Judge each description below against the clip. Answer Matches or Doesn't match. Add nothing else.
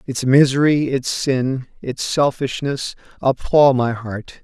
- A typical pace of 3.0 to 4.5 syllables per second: Matches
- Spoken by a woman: Doesn't match